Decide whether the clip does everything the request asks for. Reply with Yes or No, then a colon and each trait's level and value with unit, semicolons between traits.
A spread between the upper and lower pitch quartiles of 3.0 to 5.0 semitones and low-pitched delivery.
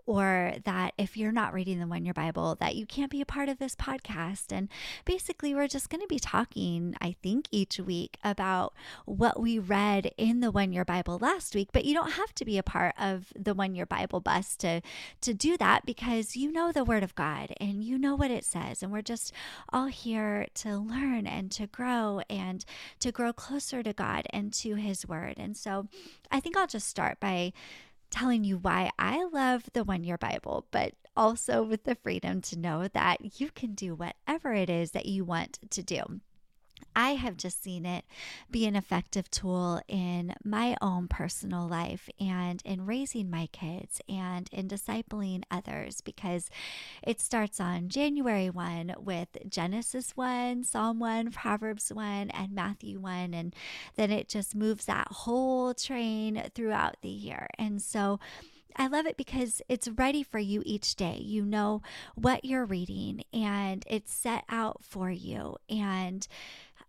No: average, 4.4 semitones; high, 210 Hz